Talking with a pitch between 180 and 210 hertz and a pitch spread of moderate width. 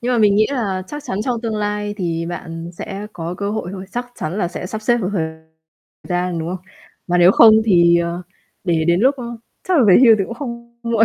Yes: high, 200 Hz; average, 4.9 semitones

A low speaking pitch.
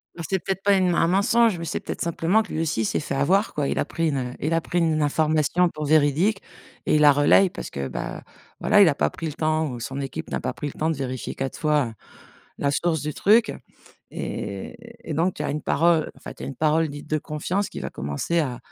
No: medium, 155 Hz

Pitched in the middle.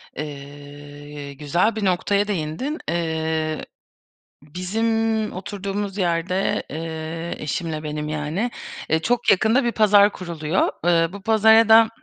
Yes: medium, 175 Hz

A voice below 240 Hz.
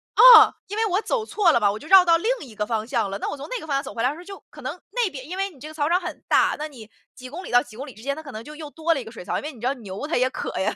No: very high, 290 Hz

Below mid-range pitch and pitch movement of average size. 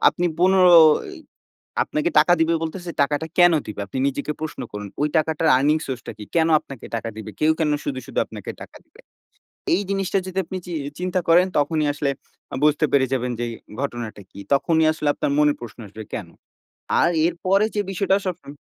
No: medium, 155 Hz; average, 4.3 semitones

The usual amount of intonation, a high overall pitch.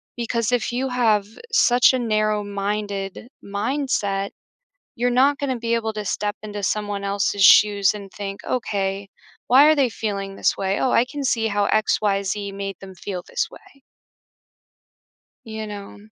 Yes: average, 3.1 semitones; high, 210 Hz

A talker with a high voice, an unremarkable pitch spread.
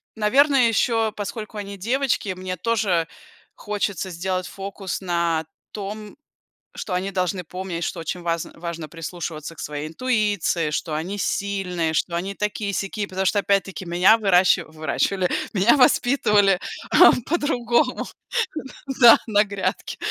Yes: high, 195 Hz; average, 3.4 semitones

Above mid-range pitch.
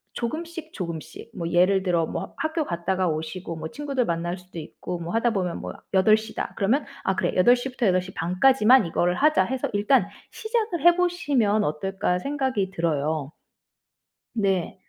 Yes: high, 195 Hz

